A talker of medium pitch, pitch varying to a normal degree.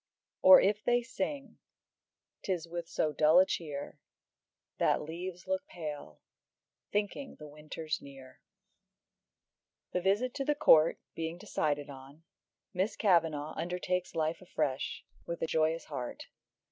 Yes: medium, 165 Hz; average, 4.1 semitones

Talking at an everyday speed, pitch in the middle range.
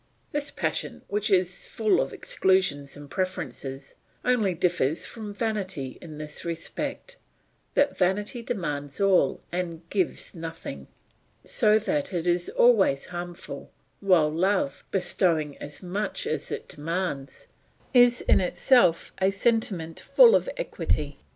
No: slow, 125 wpm; medium, 180 Hz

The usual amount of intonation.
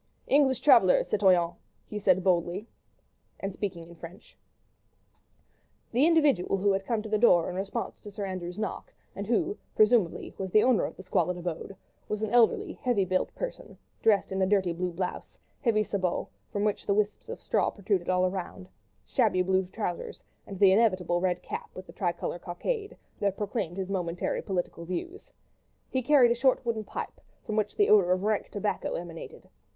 Yes: average, 3.2 semitones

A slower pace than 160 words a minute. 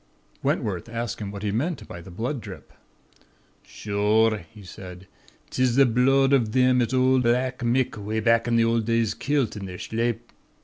No: average, 180 wpm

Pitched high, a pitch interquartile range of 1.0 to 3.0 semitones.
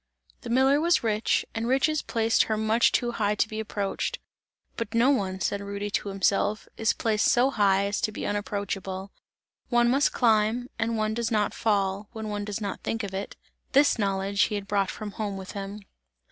Yes: high, 215 Hz; narrow, 2.4 semitones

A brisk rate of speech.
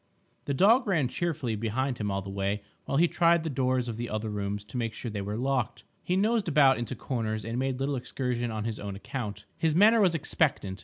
Yes: fast, 225 wpm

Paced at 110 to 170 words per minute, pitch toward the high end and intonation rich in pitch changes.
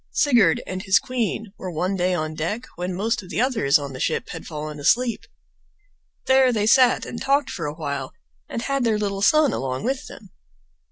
No: average, 200 wpm; high, 200 Hz; wide, 7.6 semitones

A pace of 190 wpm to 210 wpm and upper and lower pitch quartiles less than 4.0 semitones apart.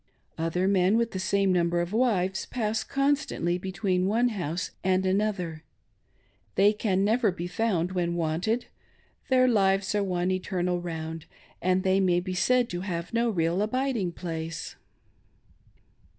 No: average, 145 wpm; average, 3.3 semitones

